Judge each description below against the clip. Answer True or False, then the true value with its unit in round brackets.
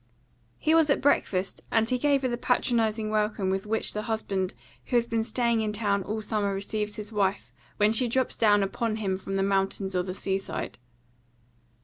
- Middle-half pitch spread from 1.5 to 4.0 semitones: True (2.8 semitones)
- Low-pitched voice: False (215 Hz)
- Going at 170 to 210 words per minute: True (200 wpm)